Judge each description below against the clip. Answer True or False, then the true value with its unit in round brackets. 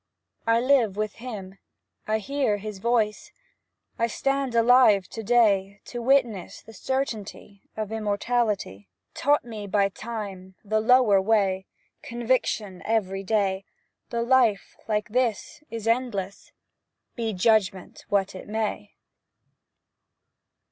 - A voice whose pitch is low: False (215 Hz)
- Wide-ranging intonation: False (3.2 semitones)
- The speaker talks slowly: True (120 wpm)